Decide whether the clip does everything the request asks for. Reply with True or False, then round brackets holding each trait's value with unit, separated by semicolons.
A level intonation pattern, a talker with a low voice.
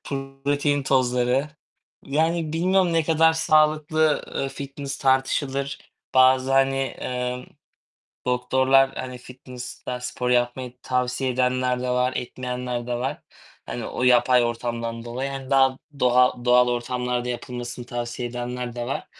True (1.7 semitones; 125 Hz)